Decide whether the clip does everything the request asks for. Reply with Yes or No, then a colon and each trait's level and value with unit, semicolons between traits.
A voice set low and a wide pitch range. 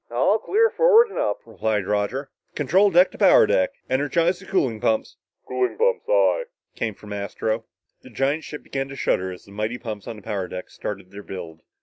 Yes: low, 115 Hz; wide, 8.4 semitones